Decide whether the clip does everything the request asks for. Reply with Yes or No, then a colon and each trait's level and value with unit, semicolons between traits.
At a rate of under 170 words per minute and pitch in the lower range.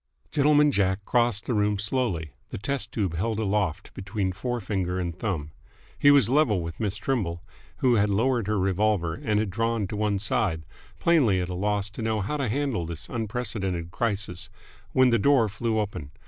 No: average, 185 wpm; low, 105 Hz